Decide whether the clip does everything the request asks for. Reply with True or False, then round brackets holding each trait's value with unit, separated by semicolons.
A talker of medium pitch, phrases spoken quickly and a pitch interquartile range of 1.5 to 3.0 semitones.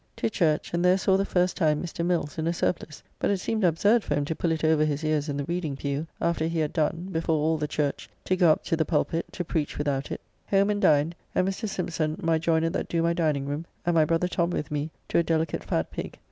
True (165 Hz; 255 wpm; 2.5 semitones)